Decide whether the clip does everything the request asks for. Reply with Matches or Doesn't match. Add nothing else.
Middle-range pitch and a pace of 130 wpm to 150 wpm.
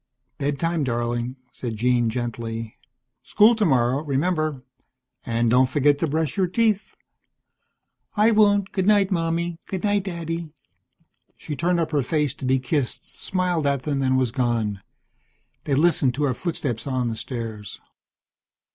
Matches